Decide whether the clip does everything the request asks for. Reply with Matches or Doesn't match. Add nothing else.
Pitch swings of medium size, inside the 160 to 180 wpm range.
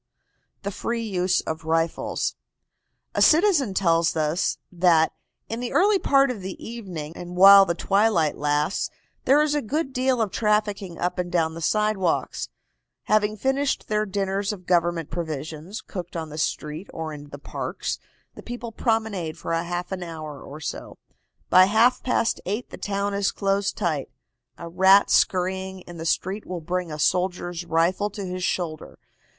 Matches